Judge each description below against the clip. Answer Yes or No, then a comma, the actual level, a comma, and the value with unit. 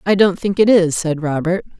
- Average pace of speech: No, fast, 235 wpm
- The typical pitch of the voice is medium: Yes, medium, 180 Hz